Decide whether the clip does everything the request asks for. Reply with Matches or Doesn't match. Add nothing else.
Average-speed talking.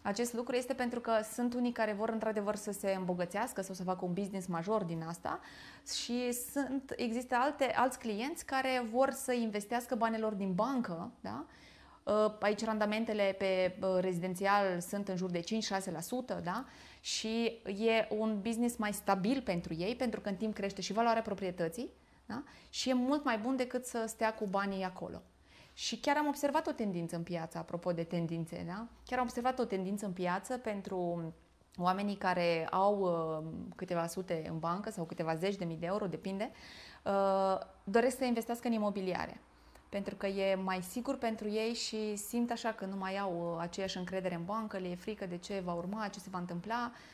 Doesn't match